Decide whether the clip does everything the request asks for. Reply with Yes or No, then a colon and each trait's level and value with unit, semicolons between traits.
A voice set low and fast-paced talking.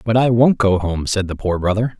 Yes: low, 105 Hz; fast, 270 wpm